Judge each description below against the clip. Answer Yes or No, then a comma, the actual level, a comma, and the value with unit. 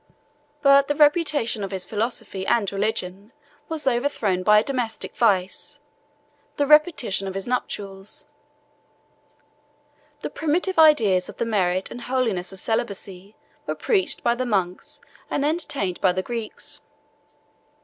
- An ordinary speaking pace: No, slow, 130 wpm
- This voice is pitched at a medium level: No, high, 225 Hz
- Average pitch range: No, wide, 6.3 semitones